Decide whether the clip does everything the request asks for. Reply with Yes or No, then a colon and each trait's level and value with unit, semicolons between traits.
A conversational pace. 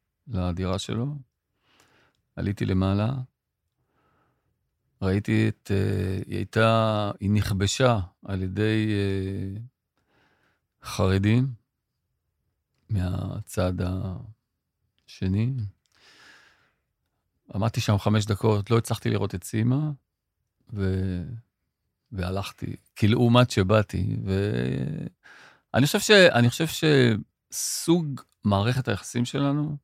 No: slow, 70 wpm